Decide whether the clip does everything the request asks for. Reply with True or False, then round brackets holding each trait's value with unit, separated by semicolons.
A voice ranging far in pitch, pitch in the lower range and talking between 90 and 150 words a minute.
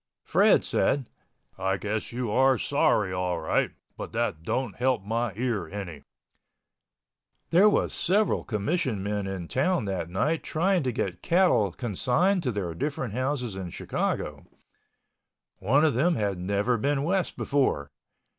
True (6.7 semitones; 120 Hz; 140 wpm)